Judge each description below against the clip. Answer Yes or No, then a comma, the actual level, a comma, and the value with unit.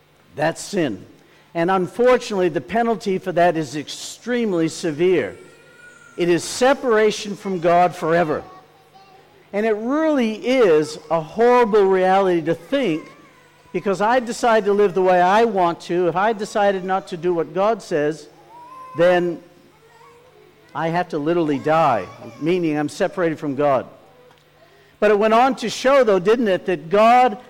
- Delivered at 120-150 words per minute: Yes, average, 145 wpm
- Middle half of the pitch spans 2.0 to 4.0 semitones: No, average, 5.0 semitones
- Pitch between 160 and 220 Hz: Yes, medium, 185 Hz